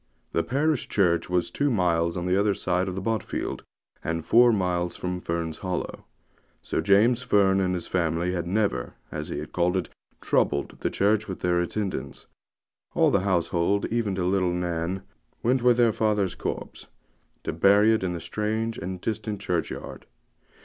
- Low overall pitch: Yes, very low, 95 Hz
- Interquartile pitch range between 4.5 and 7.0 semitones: No, average, 3.4 semitones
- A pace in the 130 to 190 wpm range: Yes, average, 165 wpm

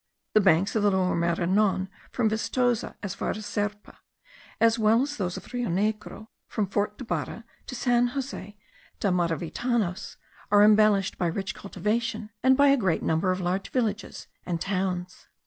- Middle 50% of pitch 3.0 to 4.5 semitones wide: Yes, average, 3.5 semitones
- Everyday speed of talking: Yes, average, 170 wpm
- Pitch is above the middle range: Yes, high, 205 Hz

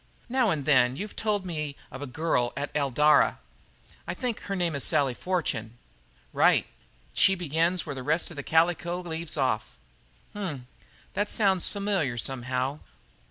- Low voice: No, medium, 155 Hz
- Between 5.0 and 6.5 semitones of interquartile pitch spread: Yes, wide, 5.4 semitones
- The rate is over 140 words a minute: Yes, average, 160 wpm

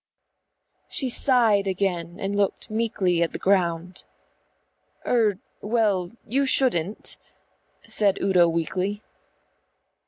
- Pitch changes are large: No, average, 3.6 semitones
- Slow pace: Yes, slow, 95 wpm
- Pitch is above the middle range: Yes, high, 195 Hz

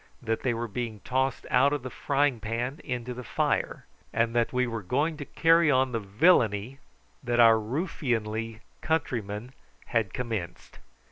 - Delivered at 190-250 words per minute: No, average, 155 wpm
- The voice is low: Yes, low, 120 Hz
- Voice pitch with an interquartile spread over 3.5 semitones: No, average, 3.0 semitones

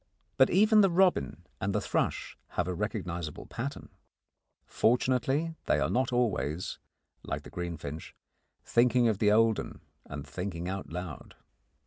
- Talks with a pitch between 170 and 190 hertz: No, low, 105 Hz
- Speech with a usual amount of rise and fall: No, wide, 6.4 semitones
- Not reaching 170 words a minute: Yes, average, 140 wpm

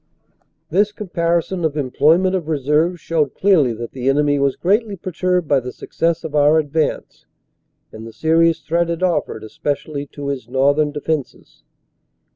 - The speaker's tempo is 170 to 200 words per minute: No, average, 150 wpm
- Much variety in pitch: No, average, 3.3 semitones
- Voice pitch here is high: No, medium, 155 Hz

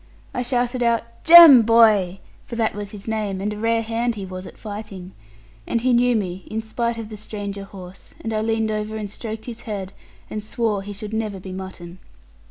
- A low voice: No, high, 215 Hz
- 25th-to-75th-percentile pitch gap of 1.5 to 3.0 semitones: Yes, narrow, 2.5 semitones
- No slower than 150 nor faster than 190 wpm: No, fast, 205 wpm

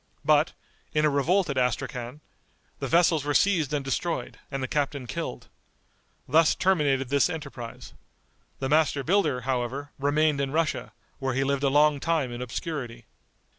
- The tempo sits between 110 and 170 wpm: Yes, average, 155 wpm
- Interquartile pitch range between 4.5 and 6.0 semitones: No, average, 2.7 semitones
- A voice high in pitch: No, medium, 140 Hz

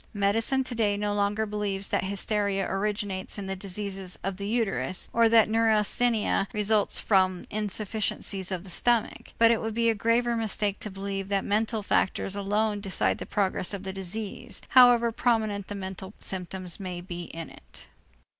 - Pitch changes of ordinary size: No, narrow, 2.3 semitones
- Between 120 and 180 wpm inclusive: Yes, average, 170 wpm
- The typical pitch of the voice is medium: No, high, 205 Hz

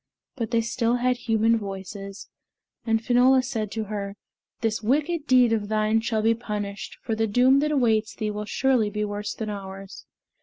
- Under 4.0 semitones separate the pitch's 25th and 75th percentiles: Yes, average, 2.8 semitones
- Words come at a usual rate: Yes, average, 180 wpm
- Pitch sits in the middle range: No, high, 225 Hz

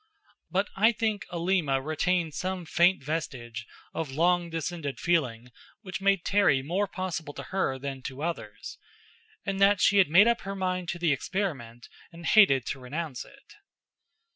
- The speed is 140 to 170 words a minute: Yes, average, 160 wpm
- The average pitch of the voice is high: No, medium, 170 Hz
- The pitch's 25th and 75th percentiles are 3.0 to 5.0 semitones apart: No, wide, 5.5 semitones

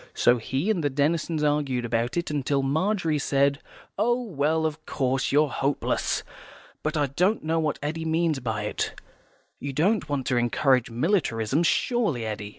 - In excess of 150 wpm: Yes, average, 160 wpm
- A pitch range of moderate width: Yes, average, 3.7 semitones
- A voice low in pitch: No, medium, 145 Hz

